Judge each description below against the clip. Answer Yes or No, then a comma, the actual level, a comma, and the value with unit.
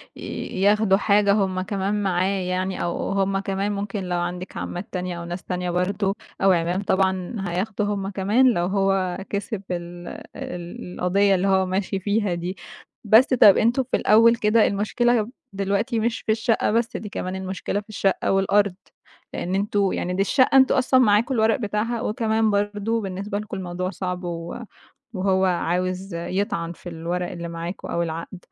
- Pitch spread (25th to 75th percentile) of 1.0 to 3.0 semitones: Yes, narrow, 2.5 semitones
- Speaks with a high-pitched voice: Yes, high, 195 Hz